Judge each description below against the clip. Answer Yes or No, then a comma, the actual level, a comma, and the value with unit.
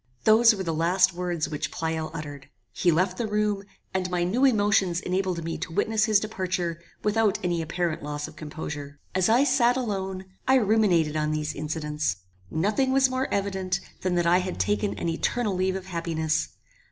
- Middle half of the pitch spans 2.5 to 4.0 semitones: No, average, 4.4 semitones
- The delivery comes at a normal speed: Yes, average, 180 wpm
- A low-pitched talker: No, medium, 185 Hz